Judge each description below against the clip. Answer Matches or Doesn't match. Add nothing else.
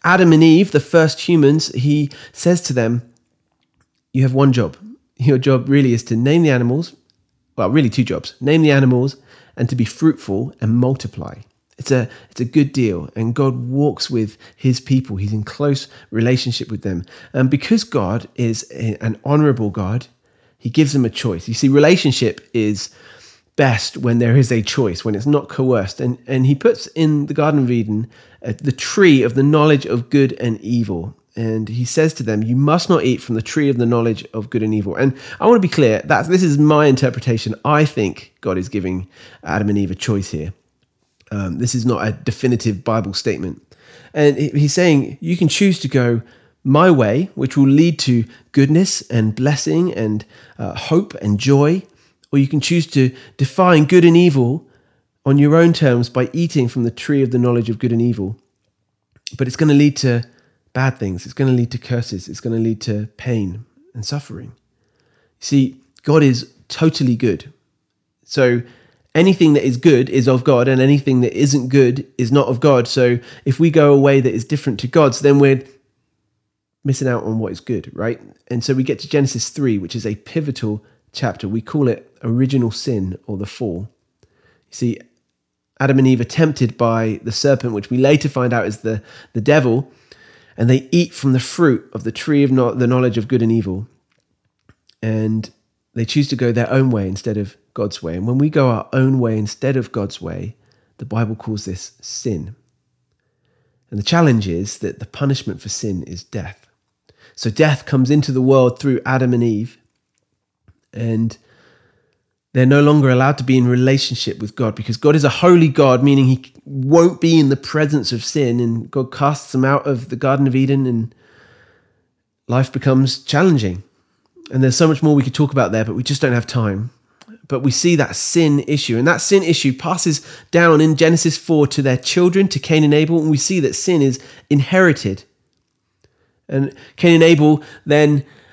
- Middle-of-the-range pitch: Doesn't match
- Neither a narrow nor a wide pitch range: Matches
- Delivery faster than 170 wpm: Matches